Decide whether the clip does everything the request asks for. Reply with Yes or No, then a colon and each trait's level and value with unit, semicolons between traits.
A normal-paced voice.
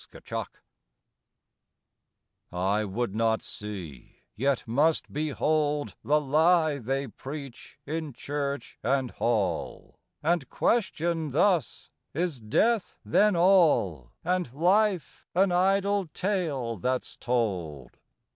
No: slow, 100 wpm